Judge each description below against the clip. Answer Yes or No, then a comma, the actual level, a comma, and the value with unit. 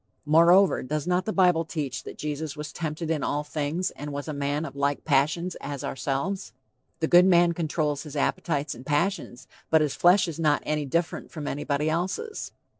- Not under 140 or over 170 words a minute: No, average, 190 wpm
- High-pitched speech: No, medium, 155 Hz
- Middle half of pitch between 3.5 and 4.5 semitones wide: No, average, 3.1 semitones